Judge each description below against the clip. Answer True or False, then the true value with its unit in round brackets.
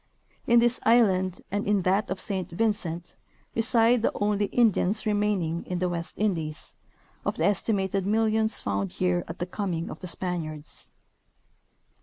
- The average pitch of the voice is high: True (195 Hz)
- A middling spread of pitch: True (3.6 semitones)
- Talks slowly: False (150 wpm)